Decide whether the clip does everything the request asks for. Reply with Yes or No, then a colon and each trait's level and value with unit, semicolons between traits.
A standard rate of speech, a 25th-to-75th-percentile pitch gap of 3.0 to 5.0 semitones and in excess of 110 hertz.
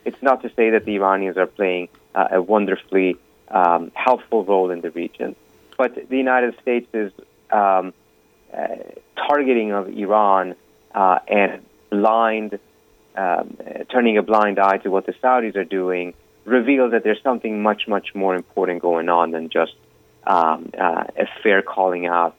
No: average, 160 wpm; average, 3.8 semitones; very low, 95 Hz